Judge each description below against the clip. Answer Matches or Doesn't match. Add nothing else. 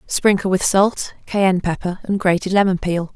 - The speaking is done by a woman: Matches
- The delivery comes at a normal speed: Matches